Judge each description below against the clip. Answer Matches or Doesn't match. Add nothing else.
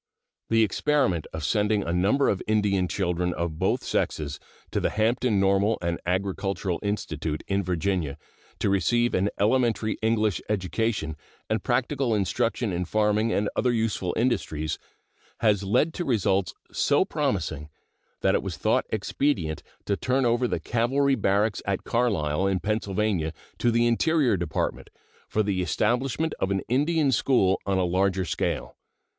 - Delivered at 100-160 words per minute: Matches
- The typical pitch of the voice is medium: Doesn't match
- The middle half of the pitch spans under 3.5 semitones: Doesn't match